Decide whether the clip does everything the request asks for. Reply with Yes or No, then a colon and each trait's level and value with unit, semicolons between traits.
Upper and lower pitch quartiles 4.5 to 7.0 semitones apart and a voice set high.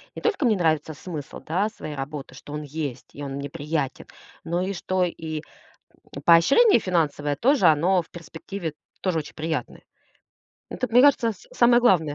No: average, 4.8 semitones; medium, 165 Hz